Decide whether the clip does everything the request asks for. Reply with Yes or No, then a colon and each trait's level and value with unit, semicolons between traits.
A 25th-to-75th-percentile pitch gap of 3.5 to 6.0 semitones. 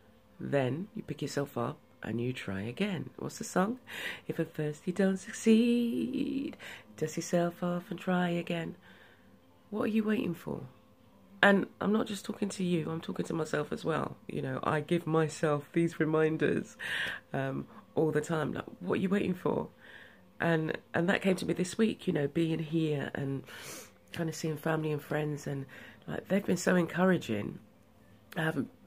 Yes: average, 4.3 semitones